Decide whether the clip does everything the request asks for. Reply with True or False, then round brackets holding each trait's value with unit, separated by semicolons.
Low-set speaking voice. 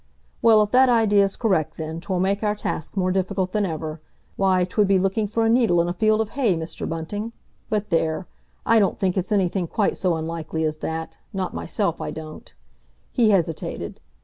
False (190 Hz)